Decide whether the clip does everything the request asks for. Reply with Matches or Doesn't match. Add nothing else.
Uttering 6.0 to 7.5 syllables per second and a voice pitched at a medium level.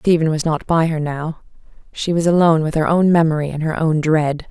Doesn't match